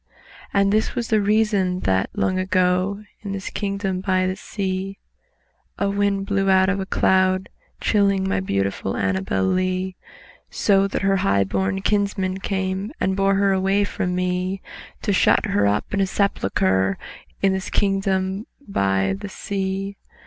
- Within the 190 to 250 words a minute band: No, average, 155 wpm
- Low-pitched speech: No, high, 190 Hz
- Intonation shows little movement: Yes, narrow, 1.5 semitones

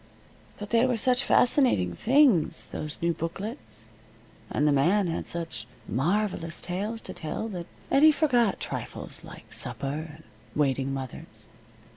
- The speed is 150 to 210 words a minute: No, slow, 135 wpm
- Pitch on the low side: No, medium, 170 Hz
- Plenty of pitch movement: Yes, wide, 7.8 semitones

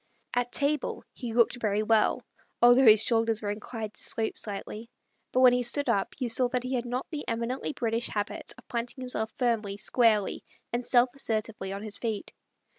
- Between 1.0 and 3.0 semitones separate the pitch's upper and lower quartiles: Yes, narrow, 2.4 semitones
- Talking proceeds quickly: No, average, 190 wpm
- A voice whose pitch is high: Yes, high, 230 Hz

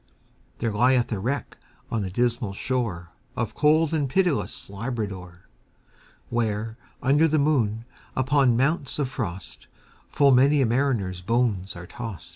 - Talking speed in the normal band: No, slow, 120 wpm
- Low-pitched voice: Yes, low, 120 Hz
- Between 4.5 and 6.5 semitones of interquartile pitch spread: Yes, average, 5.0 semitones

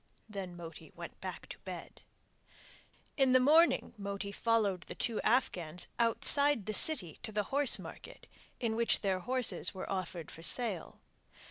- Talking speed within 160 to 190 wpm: No, average, 145 wpm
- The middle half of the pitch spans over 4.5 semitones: Yes, average, 5.2 semitones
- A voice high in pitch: Yes, high, 215 Hz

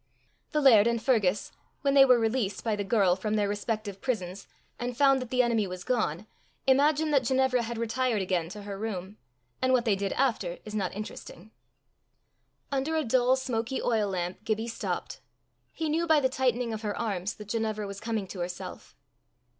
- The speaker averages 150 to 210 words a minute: Yes, average, 185 wpm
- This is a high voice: Yes, high, 225 Hz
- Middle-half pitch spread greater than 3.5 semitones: Yes, average, 4.2 semitones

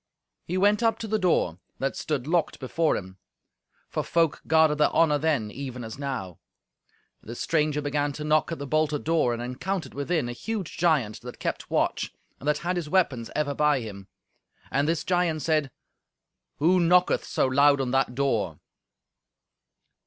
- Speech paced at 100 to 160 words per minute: No, average, 170 wpm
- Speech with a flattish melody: No, average, 4.2 semitones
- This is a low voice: No, medium, 150 Hz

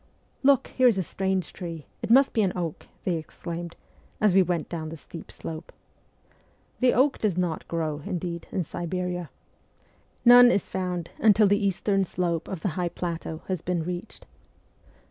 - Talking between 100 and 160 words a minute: No, average, 170 wpm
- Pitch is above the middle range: No, medium, 180 Hz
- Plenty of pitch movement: No, average, 2.8 semitones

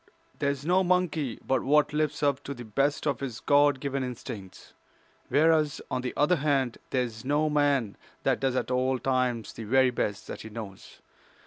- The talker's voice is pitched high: No, low, 135 Hz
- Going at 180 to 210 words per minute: Yes, average, 190 wpm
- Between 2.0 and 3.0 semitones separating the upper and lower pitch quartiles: Yes, average, 2.7 semitones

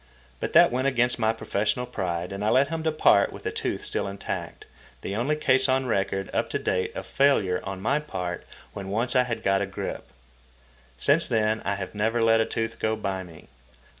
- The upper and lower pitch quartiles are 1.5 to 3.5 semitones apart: No, average, 4.5 semitones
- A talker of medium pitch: No, low, 110 Hz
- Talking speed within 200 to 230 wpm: Yes, fast, 205 wpm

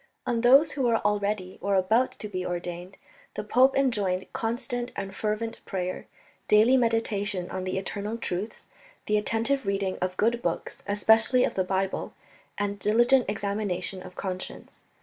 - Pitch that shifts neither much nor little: Yes, average, 3.5 semitones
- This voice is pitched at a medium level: No, high, 205 Hz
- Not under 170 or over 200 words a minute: No, average, 150 wpm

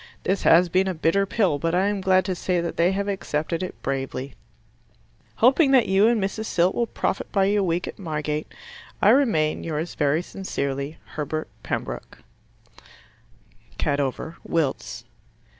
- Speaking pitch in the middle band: Yes, medium, 175 Hz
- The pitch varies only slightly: No, average, 4.3 semitones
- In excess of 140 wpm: Yes, average, 155 wpm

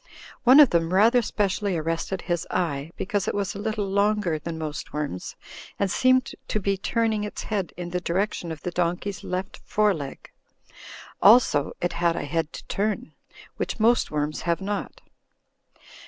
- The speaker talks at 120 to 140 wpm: No, average, 165 wpm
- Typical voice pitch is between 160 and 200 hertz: Yes, high, 190 Hz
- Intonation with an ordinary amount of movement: Yes, average, 3.9 semitones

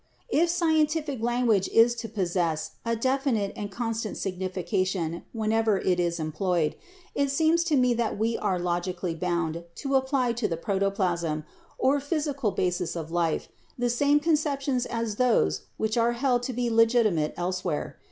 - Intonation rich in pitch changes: Yes, wide, 6.3 semitones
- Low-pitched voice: No, high, 220 Hz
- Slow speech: No, average, 155 wpm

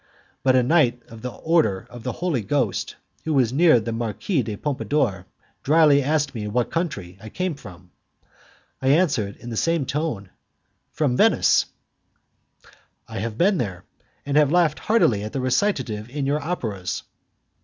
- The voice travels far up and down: Yes, wide, 6.1 semitones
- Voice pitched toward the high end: No, low, 130 Hz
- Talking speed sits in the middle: Yes, average, 160 wpm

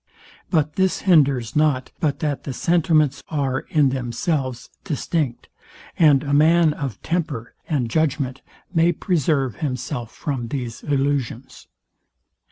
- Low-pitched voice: No, medium, 145 Hz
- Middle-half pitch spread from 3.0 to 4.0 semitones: Yes, average, 3.4 semitones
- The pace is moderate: No, slow, 120 wpm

